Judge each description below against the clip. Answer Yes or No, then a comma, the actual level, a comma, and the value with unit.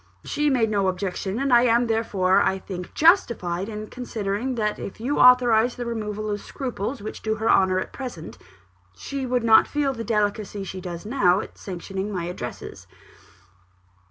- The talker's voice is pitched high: Yes, high, 215 Hz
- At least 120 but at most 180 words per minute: Yes, average, 170 wpm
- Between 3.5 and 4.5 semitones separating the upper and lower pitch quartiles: Yes, average, 4.2 semitones